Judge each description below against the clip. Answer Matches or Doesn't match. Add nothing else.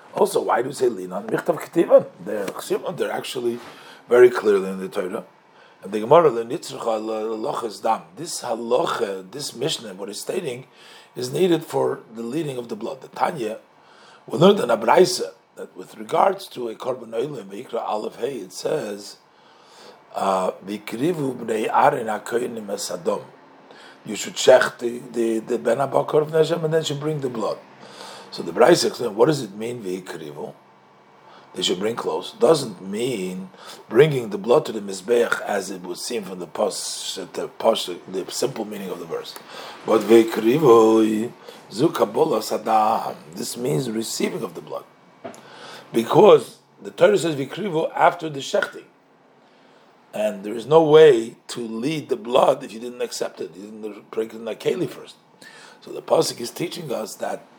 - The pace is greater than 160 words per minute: Doesn't match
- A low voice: Matches